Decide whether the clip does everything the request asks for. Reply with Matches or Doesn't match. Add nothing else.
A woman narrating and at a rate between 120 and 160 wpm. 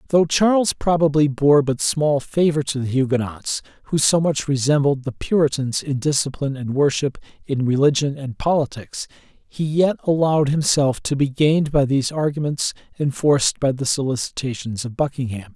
Doesn't match